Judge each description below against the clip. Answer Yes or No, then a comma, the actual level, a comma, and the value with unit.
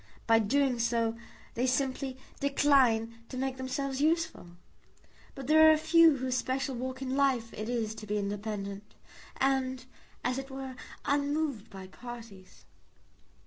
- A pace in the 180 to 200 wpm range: No, average, 145 wpm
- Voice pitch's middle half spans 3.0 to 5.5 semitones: Yes, average, 3.3 semitones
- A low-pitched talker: No, very high, 260 Hz